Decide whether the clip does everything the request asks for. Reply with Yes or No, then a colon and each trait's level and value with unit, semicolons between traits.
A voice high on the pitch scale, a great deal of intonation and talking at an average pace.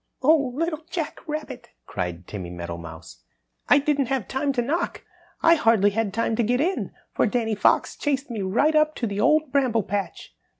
Yes: high, 245 Hz; wide, 6.6 semitones; average, 180 wpm